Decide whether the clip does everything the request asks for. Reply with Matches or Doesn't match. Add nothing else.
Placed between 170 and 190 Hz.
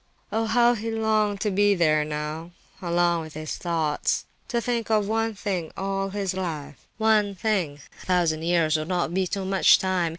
Matches